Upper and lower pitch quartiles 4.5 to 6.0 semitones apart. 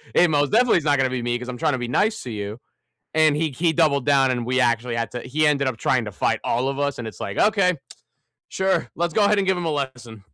Yes: average, 4.9 semitones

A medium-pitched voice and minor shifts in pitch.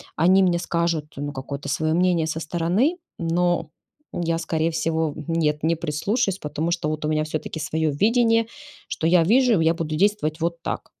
Yes: medium, 165 Hz; narrow, 2.3 semitones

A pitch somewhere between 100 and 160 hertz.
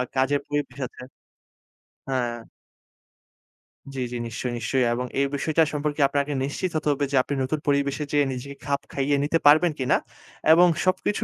Yes: medium, 140 Hz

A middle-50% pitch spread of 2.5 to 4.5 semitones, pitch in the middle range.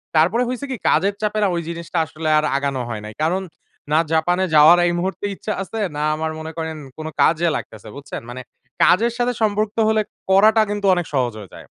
No: average, 5.1 semitones; medium, 170 Hz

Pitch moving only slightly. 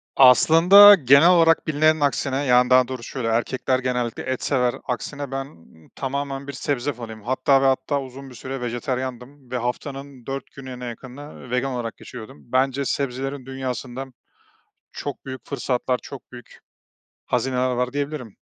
Yes: narrow, 2.0 semitones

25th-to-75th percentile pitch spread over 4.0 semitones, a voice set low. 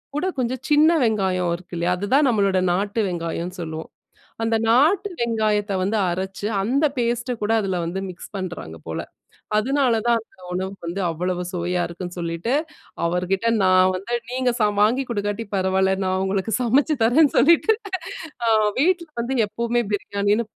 No: average, 4.7 semitones; high, 205 Hz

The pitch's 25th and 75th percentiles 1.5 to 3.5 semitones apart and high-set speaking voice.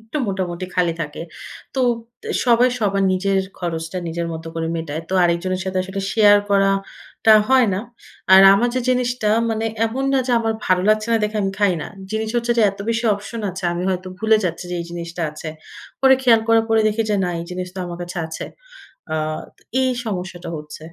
No: average, 4.1 semitones; high, 195 Hz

